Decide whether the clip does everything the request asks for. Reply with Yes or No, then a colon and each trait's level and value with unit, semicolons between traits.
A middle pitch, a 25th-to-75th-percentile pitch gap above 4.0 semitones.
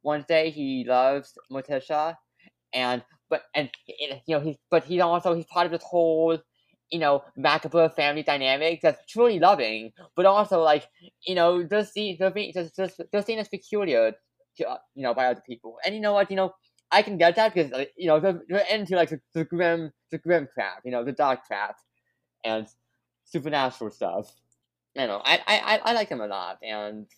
Yes: medium, 160 Hz; average, 5.1 semitones